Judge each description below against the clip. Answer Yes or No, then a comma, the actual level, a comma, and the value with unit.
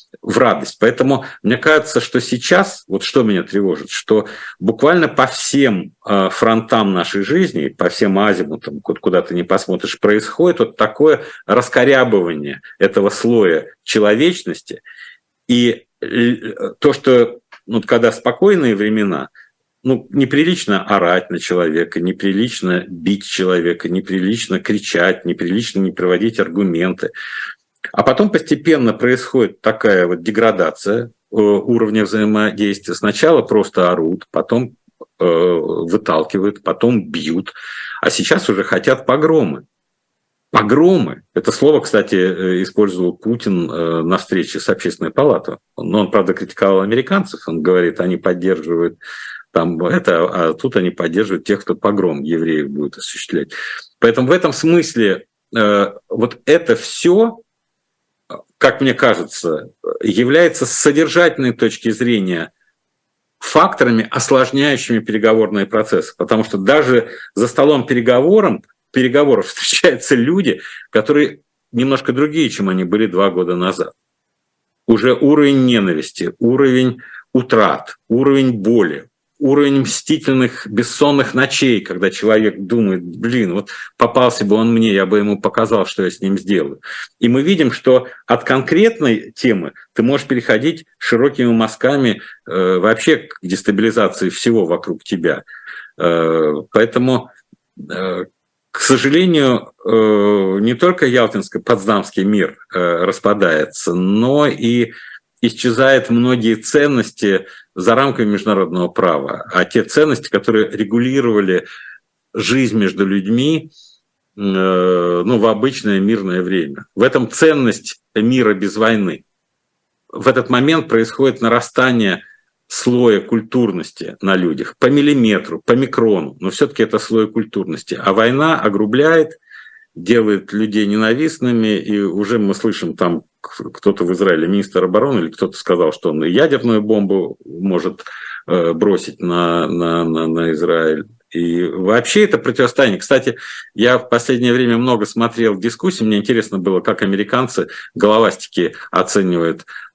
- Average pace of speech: Yes, average, 120 wpm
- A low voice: Yes, low, 115 Hz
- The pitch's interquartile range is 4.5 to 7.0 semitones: Yes, average, 5.0 semitones